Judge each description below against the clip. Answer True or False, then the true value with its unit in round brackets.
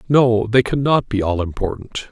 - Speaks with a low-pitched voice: True (115 Hz)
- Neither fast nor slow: True (170 wpm)